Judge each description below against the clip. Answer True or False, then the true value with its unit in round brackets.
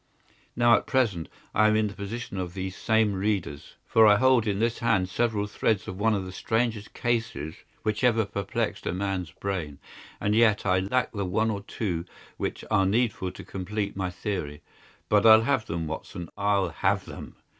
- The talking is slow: False (190 wpm)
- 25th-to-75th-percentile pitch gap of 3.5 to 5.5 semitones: False (3.0 semitones)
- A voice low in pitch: True (100 Hz)